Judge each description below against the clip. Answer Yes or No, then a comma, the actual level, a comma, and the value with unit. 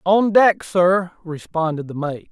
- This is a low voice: No, medium, 175 Hz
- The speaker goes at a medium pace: Yes, average, 155 wpm